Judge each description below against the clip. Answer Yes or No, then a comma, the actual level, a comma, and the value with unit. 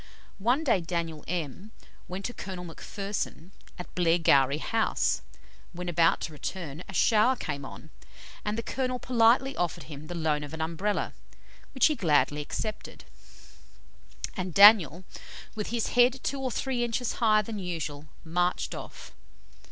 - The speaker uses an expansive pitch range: Yes, wide, 5.9 semitones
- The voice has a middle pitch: Yes, medium, 180 Hz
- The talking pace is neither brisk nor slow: Yes, average, 145 wpm